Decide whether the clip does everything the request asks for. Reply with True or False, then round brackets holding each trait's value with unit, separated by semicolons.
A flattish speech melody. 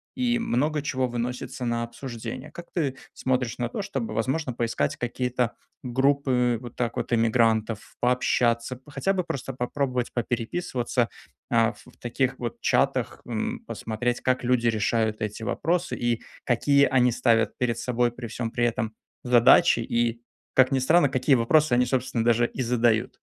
True (2.0 semitones)